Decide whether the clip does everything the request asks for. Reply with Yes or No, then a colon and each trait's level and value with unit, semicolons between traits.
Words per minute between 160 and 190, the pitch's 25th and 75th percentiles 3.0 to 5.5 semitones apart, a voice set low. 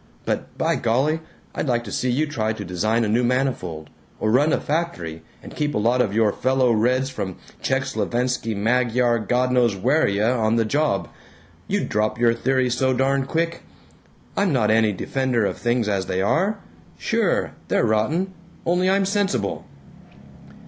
Yes: average, 165 wpm; average, 3.9 semitones; low, 120 Hz